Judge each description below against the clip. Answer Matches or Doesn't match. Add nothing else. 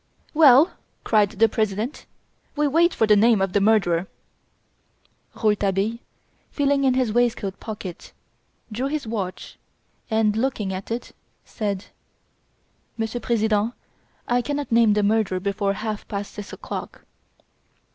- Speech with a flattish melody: Doesn't match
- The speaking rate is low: Matches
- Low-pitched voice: Doesn't match